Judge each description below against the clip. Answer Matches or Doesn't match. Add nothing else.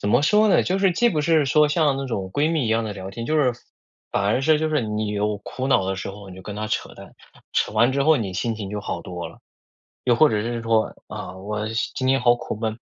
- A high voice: Doesn't match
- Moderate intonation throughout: Doesn't match